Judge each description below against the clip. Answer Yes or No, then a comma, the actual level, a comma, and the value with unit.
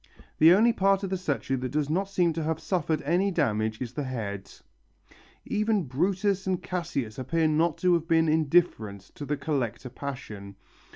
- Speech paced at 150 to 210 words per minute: Yes, average, 175 wpm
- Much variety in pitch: Yes, wide, 5.8 semitones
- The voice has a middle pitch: Yes, medium, 155 Hz